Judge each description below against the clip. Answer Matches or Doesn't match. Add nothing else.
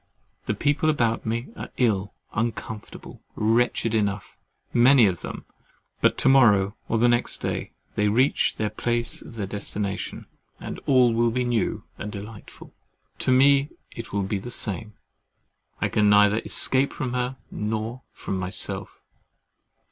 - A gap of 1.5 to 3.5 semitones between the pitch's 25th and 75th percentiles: Matches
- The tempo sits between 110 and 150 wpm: Matches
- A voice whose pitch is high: Doesn't match